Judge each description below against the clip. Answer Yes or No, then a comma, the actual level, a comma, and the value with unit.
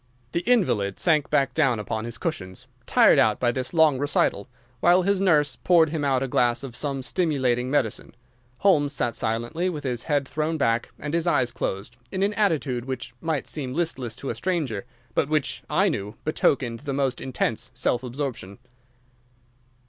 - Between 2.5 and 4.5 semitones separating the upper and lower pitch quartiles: No, average, 4.9 semitones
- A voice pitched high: No, low, 135 Hz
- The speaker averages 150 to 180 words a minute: Yes, average, 170 wpm